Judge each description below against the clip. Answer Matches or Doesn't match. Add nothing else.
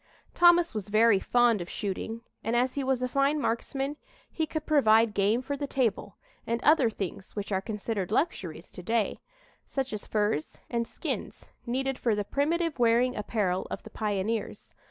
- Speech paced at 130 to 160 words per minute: Doesn't match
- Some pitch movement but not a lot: Matches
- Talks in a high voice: Matches